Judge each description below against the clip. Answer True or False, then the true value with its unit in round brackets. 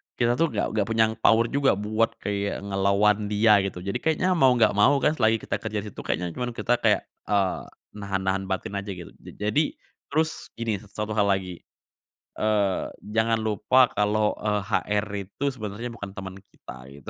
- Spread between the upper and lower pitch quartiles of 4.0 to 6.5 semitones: False (2.5 semitones)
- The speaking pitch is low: True (105 Hz)